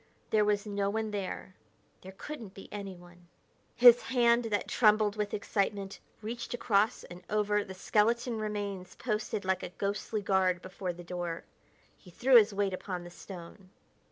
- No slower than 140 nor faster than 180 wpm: Yes, average, 155 wpm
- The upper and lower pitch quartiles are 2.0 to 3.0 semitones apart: Yes, narrow, 2.5 semitones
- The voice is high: Yes, high, 205 Hz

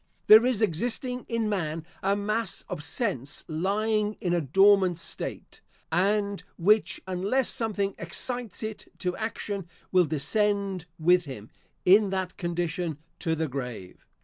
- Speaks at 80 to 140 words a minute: Yes, slow, 135 wpm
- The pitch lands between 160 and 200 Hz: Yes, high, 190 Hz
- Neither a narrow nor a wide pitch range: Yes, average, 4.1 semitones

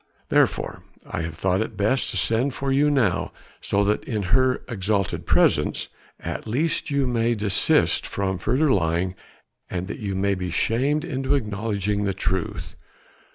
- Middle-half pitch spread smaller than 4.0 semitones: No, average, 5.3 semitones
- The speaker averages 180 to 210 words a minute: No, average, 155 wpm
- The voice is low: Yes, low, 105 Hz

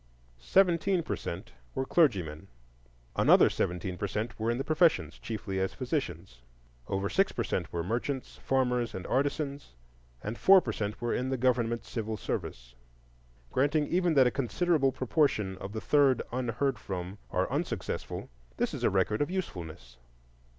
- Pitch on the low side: Yes, low, 120 Hz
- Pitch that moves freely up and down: Yes, wide, 6.6 semitones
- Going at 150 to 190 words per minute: Yes, average, 155 wpm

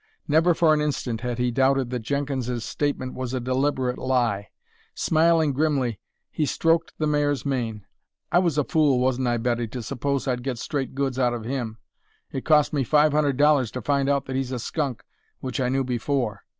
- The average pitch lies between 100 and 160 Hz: Yes, low, 135 Hz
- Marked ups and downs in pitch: No, average, 2.9 semitones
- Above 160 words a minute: Yes, average, 195 wpm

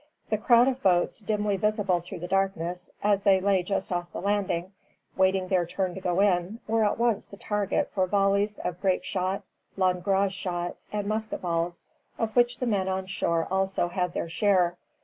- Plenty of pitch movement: No, narrow, 2.4 semitones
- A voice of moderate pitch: No, high, 195 Hz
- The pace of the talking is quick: No, average, 190 wpm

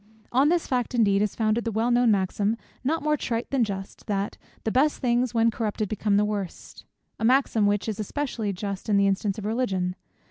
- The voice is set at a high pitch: Yes, high, 220 Hz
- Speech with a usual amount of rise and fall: Yes, average, 3.3 semitones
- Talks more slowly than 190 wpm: No, fast, 205 wpm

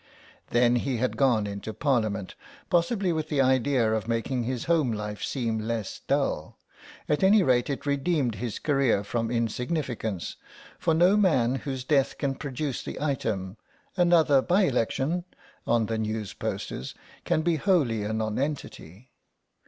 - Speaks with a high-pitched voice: No, low, 130 Hz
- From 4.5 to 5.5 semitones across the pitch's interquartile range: Yes, average, 5.2 semitones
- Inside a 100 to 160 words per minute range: Yes, average, 145 wpm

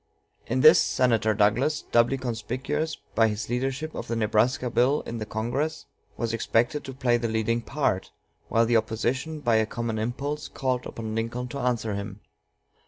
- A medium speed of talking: Yes, average, 165 wpm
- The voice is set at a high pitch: No, low, 120 Hz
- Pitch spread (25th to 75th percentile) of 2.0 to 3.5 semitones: Yes, average, 2.7 semitones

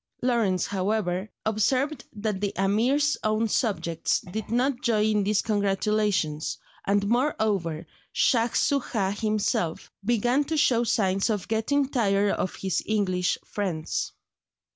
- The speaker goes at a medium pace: No, slow, 120 wpm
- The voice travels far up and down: No, average, 3.3 semitones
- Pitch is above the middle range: Yes, high, 210 Hz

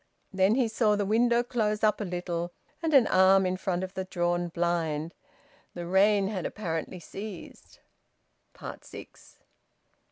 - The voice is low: No, high, 190 Hz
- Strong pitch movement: No, average, 3.4 semitones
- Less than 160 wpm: Yes, average, 140 wpm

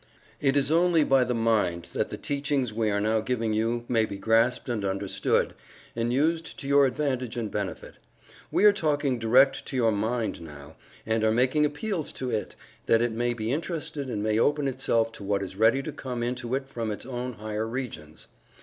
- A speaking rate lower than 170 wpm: No, average, 200 wpm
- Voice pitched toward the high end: No, low, 120 Hz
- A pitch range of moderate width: Yes, average, 3.8 semitones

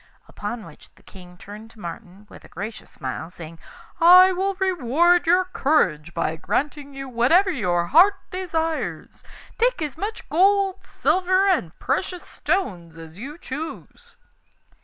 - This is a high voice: Yes, very high, 295 Hz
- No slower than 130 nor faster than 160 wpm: Yes, average, 140 wpm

